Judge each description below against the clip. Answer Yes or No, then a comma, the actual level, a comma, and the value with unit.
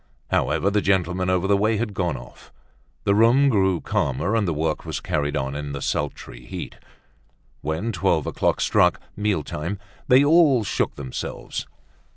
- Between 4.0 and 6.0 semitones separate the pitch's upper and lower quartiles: Yes, wide, 5.5 semitones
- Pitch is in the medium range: No, very low, 95 Hz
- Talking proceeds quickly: No, average, 155 wpm